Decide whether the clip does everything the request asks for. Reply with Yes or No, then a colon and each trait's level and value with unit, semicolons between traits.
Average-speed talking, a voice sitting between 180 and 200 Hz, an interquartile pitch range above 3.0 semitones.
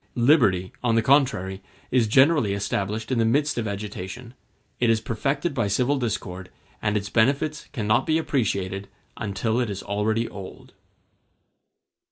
No: average, 145 wpm; low, 110 Hz; average, 4.3 semitones